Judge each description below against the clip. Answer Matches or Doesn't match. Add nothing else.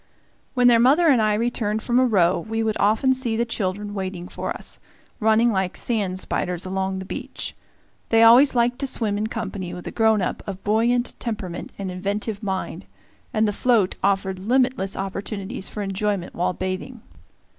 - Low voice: Doesn't match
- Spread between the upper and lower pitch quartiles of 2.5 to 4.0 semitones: Matches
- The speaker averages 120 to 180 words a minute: Matches